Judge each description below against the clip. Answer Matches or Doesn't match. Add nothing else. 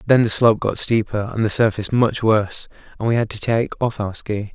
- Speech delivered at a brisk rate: Matches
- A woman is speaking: Doesn't match